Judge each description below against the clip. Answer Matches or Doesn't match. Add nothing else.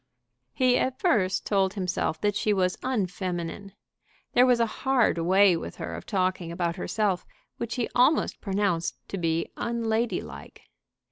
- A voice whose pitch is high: Matches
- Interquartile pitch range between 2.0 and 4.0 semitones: Doesn't match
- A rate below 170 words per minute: Matches